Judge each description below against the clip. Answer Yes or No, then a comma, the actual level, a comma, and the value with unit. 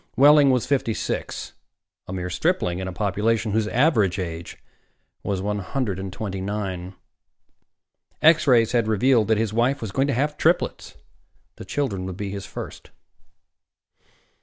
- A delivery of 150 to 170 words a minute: Yes, average, 155 wpm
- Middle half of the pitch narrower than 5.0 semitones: No, wide, 5.4 semitones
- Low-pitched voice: Yes, low, 110 Hz